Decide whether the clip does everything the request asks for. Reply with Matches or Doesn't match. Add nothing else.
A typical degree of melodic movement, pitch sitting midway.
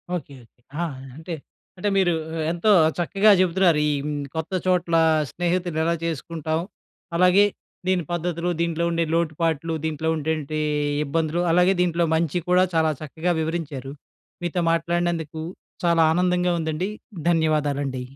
Doesn't match